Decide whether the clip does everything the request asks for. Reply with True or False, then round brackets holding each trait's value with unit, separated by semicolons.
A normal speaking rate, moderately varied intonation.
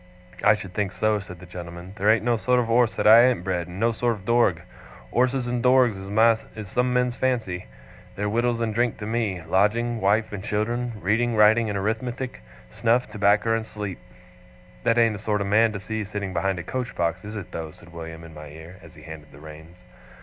False (215 wpm; 4.2 semitones)